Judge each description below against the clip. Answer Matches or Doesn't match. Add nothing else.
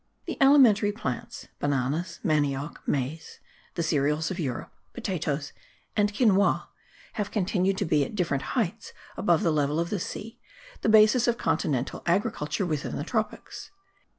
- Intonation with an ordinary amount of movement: Doesn't match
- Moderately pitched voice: Matches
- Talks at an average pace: Matches